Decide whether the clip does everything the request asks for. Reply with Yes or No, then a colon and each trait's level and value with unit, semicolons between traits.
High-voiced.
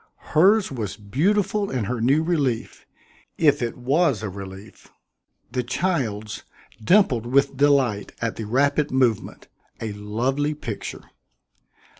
No: low, 130 Hz